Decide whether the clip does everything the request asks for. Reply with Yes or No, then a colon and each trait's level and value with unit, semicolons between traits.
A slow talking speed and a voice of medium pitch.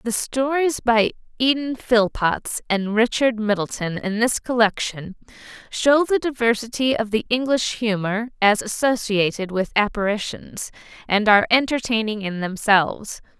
No: slow, 120 wpm; high, 225 Hz